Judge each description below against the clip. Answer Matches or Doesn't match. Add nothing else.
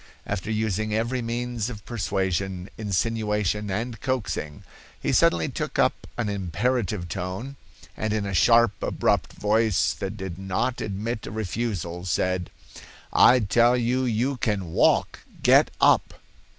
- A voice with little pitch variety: Doesn't match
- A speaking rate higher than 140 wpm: Doesn't match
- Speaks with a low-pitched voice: Matches